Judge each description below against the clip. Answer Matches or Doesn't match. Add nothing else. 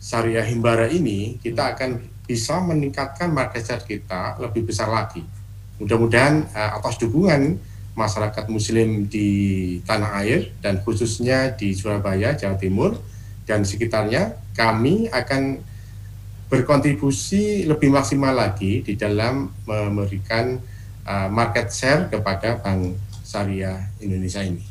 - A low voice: Matches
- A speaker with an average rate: Matches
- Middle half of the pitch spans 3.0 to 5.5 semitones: Matches